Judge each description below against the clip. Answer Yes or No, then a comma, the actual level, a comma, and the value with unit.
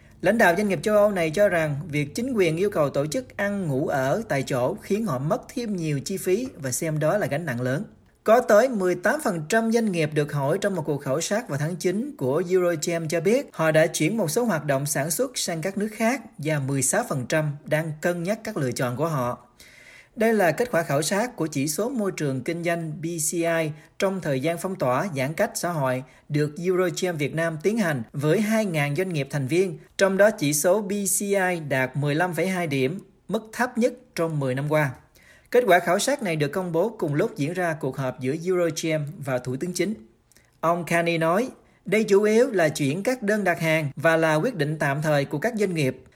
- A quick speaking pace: No, average, 220 wpm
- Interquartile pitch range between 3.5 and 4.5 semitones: No, average, 5.2 semitones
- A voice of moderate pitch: Yes, medium, 170 Hz